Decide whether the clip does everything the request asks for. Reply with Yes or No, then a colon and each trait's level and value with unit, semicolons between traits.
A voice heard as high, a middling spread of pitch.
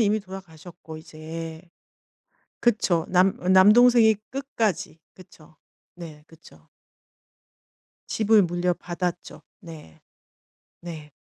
No: medium, 175 Hz; average, 4.0 semitones